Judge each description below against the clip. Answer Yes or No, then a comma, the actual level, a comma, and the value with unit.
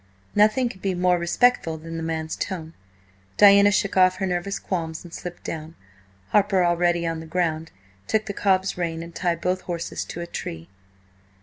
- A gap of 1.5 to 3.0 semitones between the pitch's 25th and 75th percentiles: Yes, narrow, 2.6 semitones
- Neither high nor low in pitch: Yes, medium, 175 Hz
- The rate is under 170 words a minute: No, average, 180 wpm